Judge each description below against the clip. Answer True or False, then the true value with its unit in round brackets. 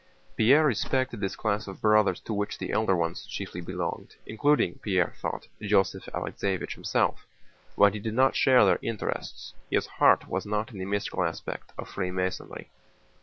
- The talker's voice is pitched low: True (105 Hz)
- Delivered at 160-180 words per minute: True (165 wpm)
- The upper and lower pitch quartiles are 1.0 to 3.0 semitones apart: True (2.7 semitones)